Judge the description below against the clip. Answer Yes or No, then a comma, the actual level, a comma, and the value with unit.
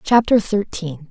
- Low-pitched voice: No, high, 190 Hz